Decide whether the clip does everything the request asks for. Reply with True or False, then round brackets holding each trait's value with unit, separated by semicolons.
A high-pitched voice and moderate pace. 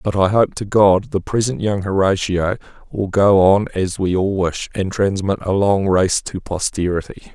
False (95 Hz; 190 wpm)